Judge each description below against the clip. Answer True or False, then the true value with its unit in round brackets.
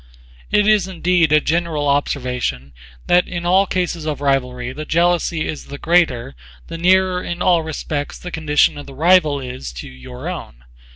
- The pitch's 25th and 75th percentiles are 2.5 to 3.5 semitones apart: False (4.4 semitones)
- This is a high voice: False (155 Hz)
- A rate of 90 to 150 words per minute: False (170 wpm)